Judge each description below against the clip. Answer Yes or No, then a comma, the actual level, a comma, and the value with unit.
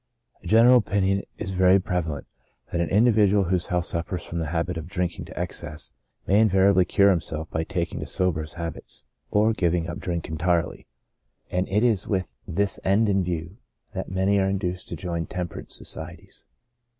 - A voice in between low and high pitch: No, very low, 90 Hz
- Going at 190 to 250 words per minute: No, average, 175 wpm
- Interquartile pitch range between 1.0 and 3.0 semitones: Yes, narrow, 2.6 semitones